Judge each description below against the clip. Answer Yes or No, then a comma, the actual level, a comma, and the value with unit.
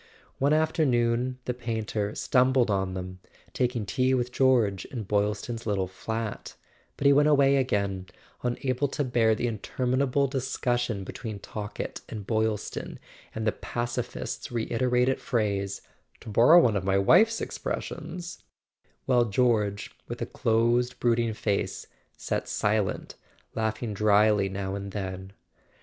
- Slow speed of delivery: Yes, slow, 130 wpm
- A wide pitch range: No, average, 3.6 semitones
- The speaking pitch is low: Yes, low, 115 Hz